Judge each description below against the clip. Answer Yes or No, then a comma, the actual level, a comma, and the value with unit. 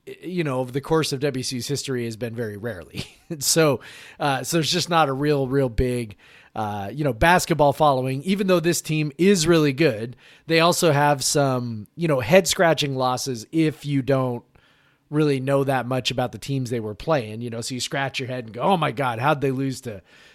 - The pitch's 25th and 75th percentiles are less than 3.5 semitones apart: No, average, 3.9 semitones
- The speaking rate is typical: No, fast, 210 wpm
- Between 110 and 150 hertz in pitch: Yes, medium, 140 Hz